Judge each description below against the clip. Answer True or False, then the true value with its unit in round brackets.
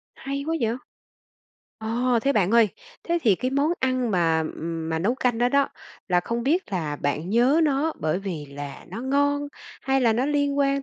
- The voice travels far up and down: True (7.5 semitones)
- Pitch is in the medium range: False (240 Hz)